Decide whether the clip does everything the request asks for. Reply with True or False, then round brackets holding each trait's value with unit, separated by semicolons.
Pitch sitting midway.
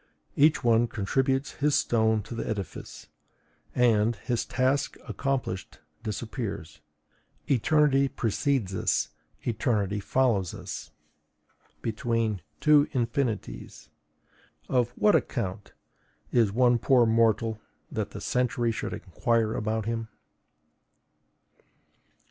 False (115 Hz)